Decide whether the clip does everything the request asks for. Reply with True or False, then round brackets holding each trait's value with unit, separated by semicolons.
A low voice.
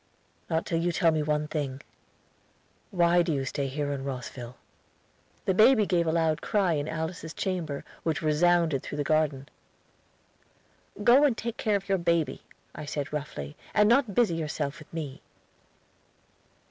False (160 Hz)